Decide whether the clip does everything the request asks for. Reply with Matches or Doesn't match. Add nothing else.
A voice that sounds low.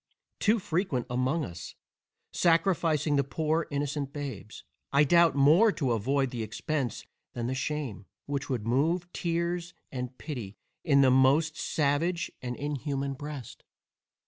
Doesn't match